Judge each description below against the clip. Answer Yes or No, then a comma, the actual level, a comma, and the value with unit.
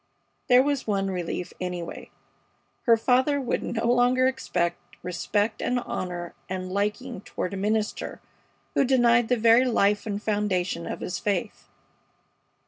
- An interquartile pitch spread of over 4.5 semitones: Yes, average, 4.9 semitones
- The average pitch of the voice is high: Yes, high, 215 Hz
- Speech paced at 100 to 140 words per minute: Yes, slow, 135 wpm